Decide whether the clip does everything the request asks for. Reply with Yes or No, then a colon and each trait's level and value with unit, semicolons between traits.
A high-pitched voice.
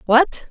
Yes: very high, 285 Hz